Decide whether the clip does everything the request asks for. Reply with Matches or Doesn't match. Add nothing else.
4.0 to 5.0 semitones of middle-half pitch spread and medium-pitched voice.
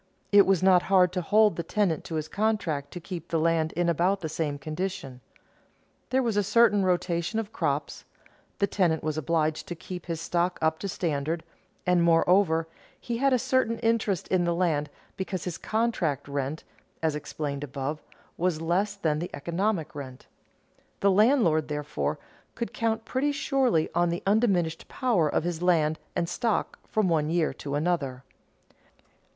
Matches